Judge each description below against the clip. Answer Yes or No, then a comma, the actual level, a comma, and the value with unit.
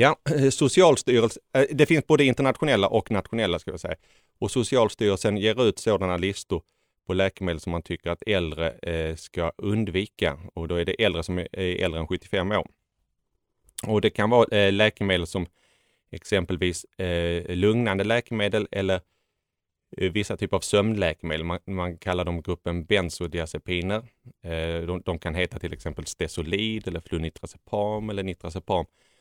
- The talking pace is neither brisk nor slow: Yes, average, 135 wpm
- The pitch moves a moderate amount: Yes, average, 3.6 semitones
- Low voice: Yes, very low, 95 Hz